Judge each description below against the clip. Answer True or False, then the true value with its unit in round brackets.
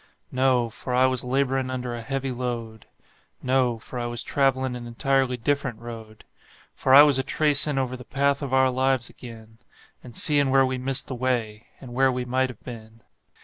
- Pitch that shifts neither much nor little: False (2.0 semitones)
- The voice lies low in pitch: True (130 Hz)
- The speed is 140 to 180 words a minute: False (190 wpm)